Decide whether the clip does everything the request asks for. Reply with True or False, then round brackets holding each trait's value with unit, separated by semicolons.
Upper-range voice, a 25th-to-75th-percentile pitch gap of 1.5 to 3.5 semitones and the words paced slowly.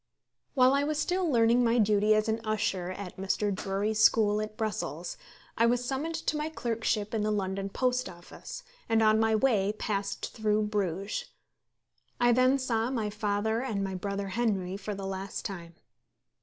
False (215 Hz; 3.1 semitones; 170 wpm)